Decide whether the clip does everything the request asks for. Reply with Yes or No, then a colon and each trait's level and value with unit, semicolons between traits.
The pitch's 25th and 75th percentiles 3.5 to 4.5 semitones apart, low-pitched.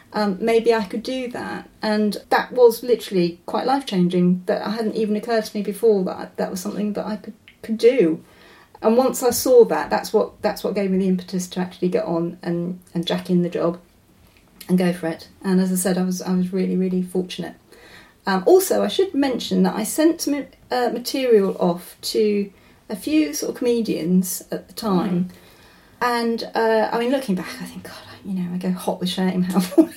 No: average, 4.1 semitones; high, 205 Hz